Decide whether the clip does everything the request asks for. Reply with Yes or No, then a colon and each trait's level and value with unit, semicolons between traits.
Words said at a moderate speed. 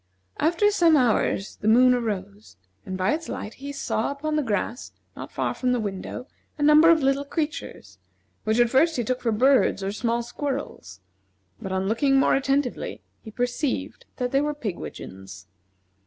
Yes: average, 170 wpm